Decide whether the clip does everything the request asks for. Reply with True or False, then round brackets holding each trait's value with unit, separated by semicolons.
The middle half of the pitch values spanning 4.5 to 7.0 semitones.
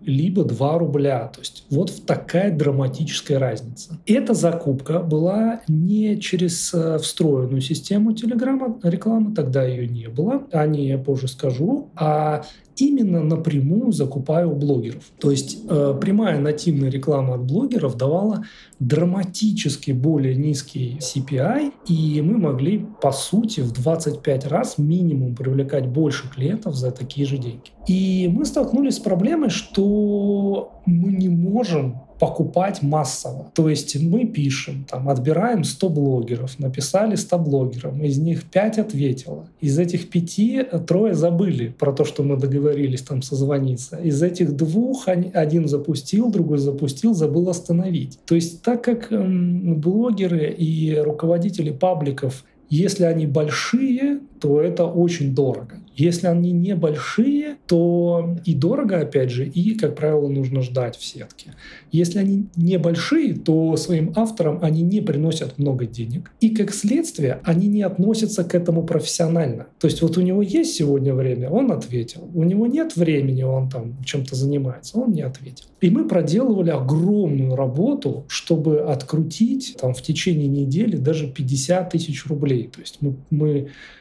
True (5.2 semitones)